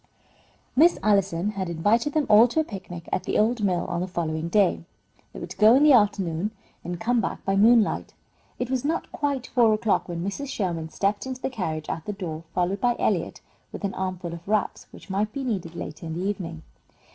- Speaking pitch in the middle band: No, high, 200 Hz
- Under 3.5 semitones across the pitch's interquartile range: No, average, 5.1 semitones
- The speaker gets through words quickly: Yes, fast, 215 wpm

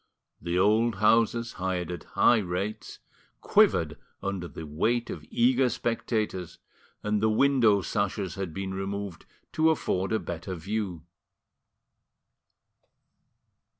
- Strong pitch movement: No, average, 3.8 semitones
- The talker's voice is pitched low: Yes, low, 100 Hz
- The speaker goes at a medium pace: No, slow, 115 wpm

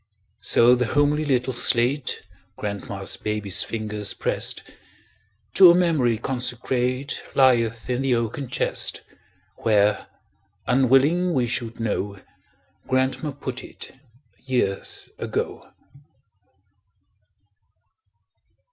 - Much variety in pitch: No, average, 3.1 semitones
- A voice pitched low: Yes, low, 125 Hz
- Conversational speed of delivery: No, slow, 90 wpm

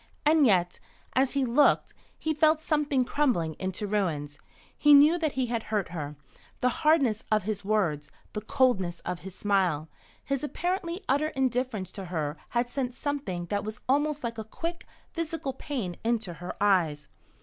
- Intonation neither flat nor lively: No, wide, 7.4 semitones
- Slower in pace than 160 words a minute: No, average, 165 wpm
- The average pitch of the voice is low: No, high, 235 Hz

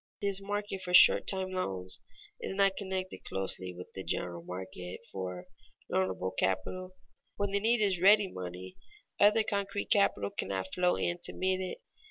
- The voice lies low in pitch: No, medium, 185 Hz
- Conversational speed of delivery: Yes, average, 165 wpm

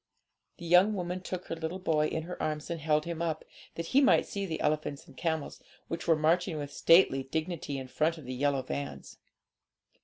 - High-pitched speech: No, medium, 160 Hz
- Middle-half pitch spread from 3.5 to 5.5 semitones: No, average, 2.7 semitones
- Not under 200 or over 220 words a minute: Yes, fast, 205 wpm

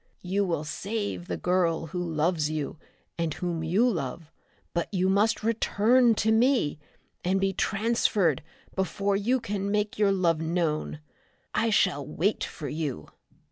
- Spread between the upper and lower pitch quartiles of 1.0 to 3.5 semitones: No, average, 4.3 semitones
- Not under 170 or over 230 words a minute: No, average, 145 wpm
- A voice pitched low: No, medium, 185 Hz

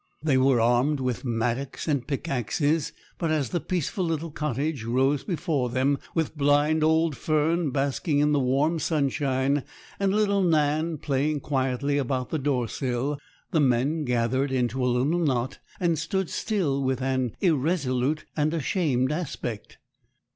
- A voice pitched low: No, medium, 145 Hz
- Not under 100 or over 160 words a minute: Yes, average, 145 wpm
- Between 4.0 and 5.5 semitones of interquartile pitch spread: No, average, 3.4 semitones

